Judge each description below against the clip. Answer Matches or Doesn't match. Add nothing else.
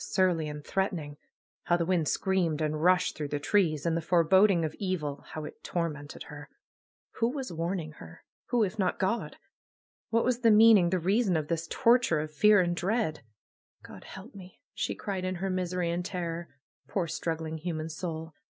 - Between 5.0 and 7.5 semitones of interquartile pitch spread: Doesn't match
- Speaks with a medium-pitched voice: Matches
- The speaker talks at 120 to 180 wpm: Doesn't match